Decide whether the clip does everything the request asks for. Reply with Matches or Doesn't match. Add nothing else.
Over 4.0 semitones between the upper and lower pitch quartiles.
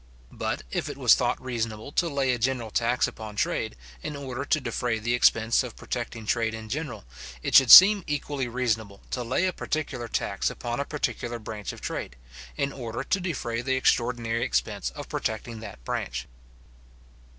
Doesn't match